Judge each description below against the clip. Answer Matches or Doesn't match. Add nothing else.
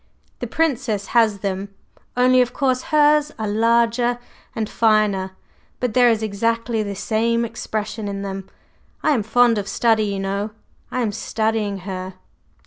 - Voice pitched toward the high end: Matches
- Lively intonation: Doesn't match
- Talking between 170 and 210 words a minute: Doesn't match